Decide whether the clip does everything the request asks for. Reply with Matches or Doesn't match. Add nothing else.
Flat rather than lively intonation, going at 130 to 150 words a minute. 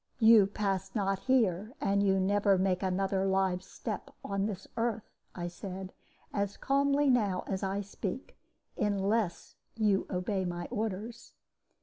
Matches